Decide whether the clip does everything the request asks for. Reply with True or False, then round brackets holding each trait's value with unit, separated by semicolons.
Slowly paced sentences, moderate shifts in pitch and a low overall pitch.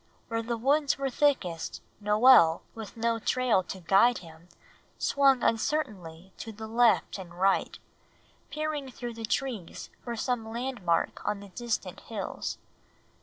False (130 wpm; 4.8 semitones; 225 Hz)